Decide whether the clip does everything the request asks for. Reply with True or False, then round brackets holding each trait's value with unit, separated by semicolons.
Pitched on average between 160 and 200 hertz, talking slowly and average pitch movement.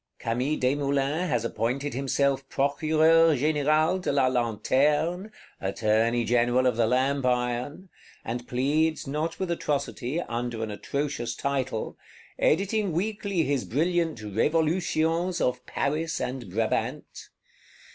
False (140 Hz; 115 wpm; 4.7 semitones)